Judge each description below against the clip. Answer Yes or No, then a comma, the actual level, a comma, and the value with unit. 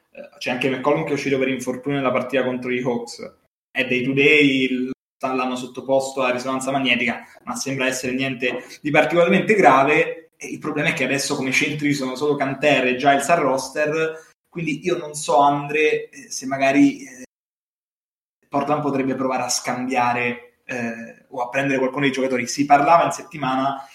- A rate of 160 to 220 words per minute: Yes, fast, 170 wpm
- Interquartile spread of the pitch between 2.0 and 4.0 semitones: Yes, average, 2.7 semitones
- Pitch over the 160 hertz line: No, low, 135 Hz